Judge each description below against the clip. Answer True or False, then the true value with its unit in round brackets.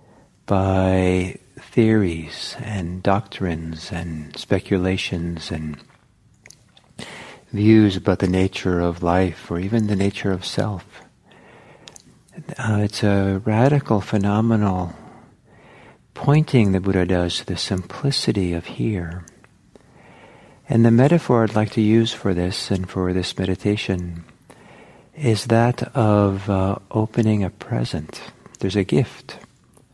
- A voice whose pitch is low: True (100 Hz)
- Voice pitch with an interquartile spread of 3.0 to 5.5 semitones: True (3.4 semitones)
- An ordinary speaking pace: False (110 wpm)